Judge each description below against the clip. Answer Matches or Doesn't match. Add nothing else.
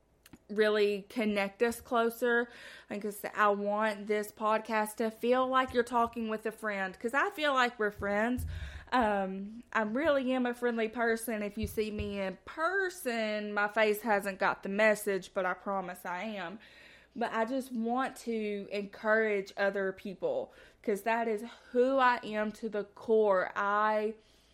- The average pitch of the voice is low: Doesn't match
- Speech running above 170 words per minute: Doesn't match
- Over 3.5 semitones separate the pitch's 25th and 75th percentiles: Doesn't match